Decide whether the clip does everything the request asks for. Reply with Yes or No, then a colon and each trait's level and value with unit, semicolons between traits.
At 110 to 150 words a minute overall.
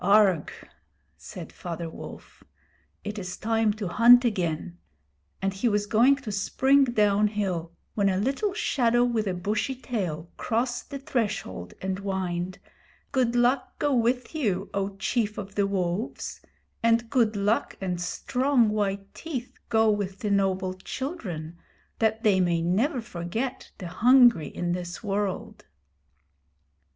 Yes: average, 140 wpm